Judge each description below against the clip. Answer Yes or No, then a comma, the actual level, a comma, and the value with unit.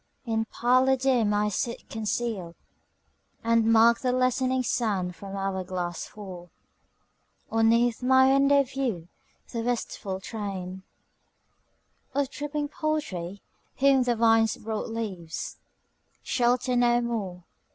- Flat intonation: No, average, 4.4 semitones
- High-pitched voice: Yes, high, 230 Hz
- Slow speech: Yes, slow, 115 wpm